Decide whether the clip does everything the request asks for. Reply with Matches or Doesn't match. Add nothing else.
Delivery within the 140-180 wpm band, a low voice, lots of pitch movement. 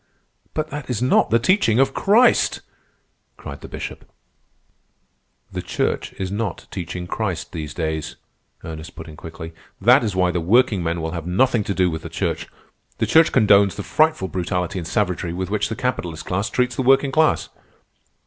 Matches